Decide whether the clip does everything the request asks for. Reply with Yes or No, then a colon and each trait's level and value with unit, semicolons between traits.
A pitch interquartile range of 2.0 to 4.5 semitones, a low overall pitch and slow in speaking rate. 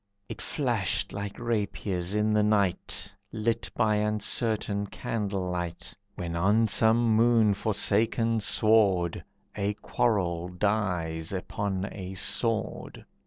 Yes: average, 2.9 semitones; low, 105 Hz; slow, 110 wpm